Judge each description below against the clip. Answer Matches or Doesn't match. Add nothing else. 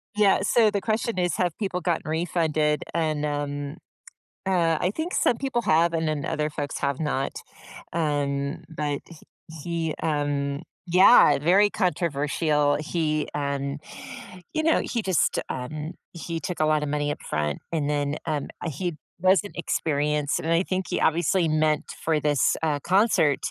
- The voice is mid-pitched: Matches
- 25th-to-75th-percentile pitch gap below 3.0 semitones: Doesn't match